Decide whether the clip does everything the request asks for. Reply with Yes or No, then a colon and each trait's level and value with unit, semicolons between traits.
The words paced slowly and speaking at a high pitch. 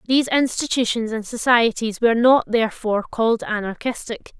Yes: slow, 125 wpm; high, 230 Hz